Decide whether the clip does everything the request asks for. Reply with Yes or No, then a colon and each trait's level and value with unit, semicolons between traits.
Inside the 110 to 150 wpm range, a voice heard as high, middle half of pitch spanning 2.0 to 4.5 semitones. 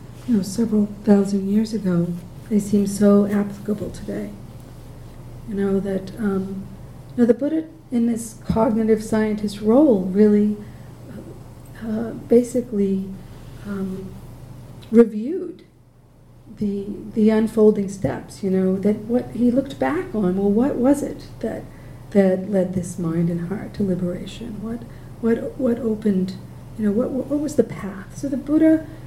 Yes: average, 140 wpm; high, 210 Hz; average, 3.5 semitones